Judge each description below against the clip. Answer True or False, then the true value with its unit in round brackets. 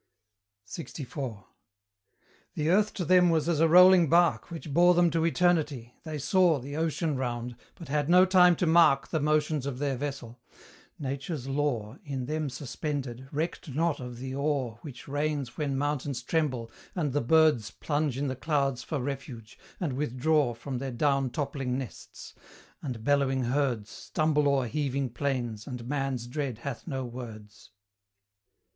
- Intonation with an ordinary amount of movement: True (3.6 semitones)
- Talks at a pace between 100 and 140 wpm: False (155 wpm)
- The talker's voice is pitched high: False (140 Hz)